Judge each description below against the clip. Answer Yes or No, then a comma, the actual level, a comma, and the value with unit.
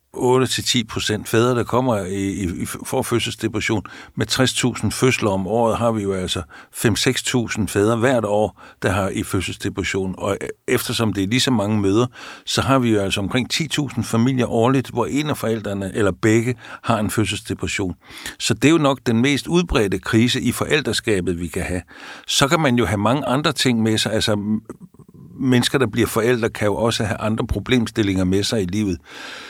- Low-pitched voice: Yes, low, 115 Hz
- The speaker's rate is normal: Yes, average, 180 wpm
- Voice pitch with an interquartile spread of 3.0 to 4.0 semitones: Yes, average, 3.6 semitones